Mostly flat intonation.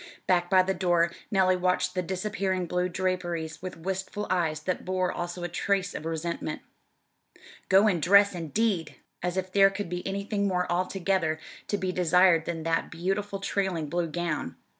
Yes: narrow, 1.9 semitones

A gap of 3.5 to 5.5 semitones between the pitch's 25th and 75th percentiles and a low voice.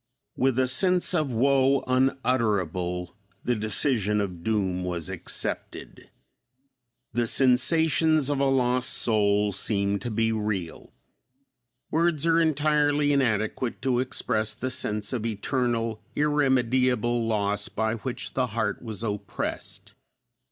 Yes: average, 4.3 semitones; low, 120 Hz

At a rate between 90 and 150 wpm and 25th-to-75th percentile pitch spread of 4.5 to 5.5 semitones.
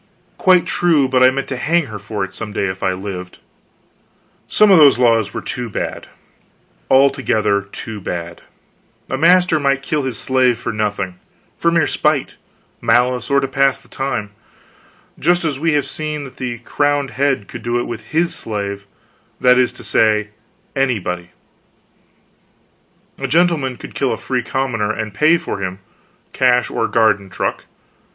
No: average, 165 wpm; average, 5.1 semitones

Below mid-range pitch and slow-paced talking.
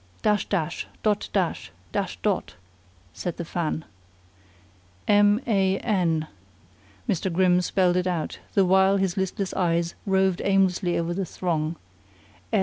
No: medium, 185 Hz; slow, 130 wpm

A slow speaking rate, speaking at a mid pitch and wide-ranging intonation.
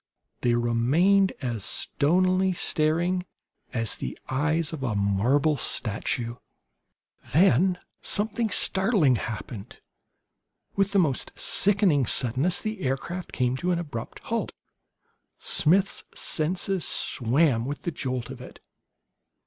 Yes: slow, 110 wpm; medium, 155 Hz; wide, 7.0 semitones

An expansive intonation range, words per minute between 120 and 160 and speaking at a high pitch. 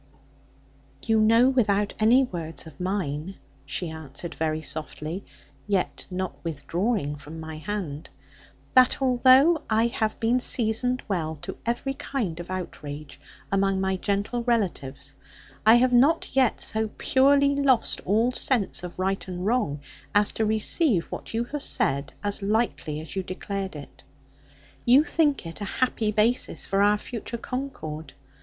Yes: wide, 6.4 semitones; average, 145 wpm; high, 205 Hz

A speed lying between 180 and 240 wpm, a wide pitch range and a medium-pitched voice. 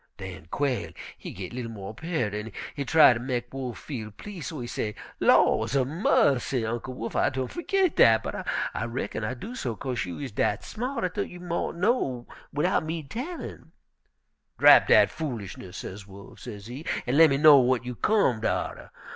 No: average, 185 wpm; wide, 6.0 semitones; low, 130 Hz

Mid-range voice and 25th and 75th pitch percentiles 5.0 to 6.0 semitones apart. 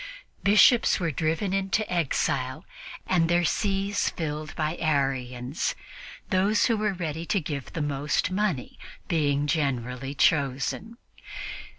Yes: medium, 160 Hz; wide, 5.5 semitones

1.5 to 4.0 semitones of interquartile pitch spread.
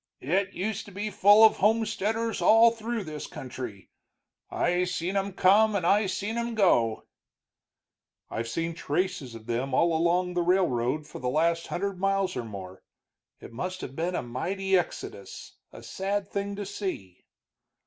No: wide, 5.4 semitones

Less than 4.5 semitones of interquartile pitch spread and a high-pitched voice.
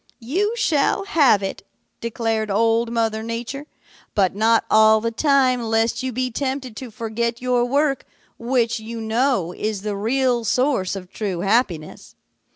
Yes: average, 2.9 semitones; high, 230 Hz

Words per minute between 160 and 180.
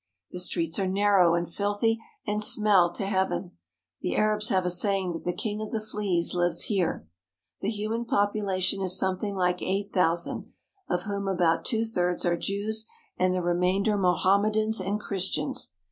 Yes: average, 165 wpm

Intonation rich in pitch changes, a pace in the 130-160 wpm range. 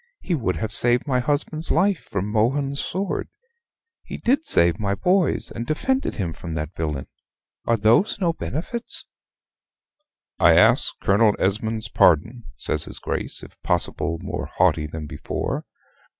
Yes: wide, 8.9 semitones; average, 145 wpm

